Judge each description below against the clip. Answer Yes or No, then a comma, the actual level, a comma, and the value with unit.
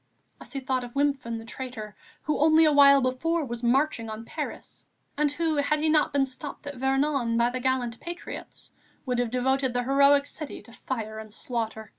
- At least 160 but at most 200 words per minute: Yes, average, 195 wpm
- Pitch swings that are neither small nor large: Yes, average, 3.2 semitones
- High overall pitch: Yes, very high, 265 Hz